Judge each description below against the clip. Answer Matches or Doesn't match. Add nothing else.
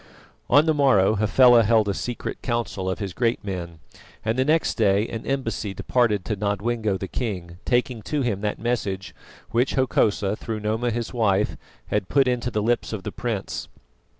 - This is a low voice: Matches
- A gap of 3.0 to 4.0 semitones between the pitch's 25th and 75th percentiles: Matches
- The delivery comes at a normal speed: Matches